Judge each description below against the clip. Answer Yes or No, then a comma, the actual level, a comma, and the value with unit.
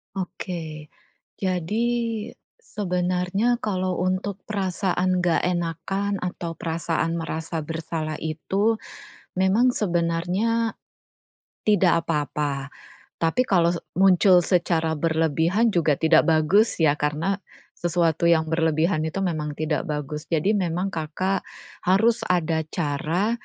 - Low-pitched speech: No, medium, 170 Hz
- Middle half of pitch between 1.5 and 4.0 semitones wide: Yes, average, 3.0 semitones